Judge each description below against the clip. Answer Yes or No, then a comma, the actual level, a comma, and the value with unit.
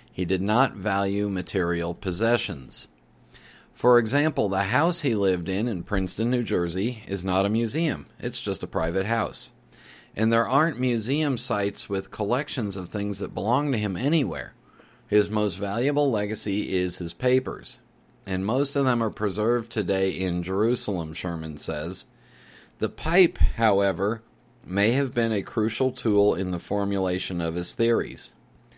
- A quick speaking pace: No, average, 150 wpm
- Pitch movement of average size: Yes, average, 4.2 semitones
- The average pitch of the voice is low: Yes, low, 105 Hz